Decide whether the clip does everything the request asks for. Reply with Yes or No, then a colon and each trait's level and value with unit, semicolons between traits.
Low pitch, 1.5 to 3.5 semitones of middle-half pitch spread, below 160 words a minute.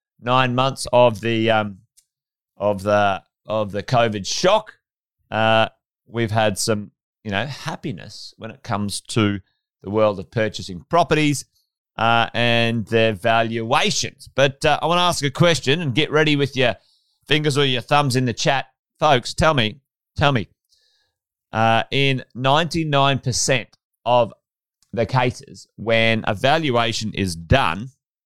No: low, 120 Hz; average, 4.2 semitones; average, 140 wpm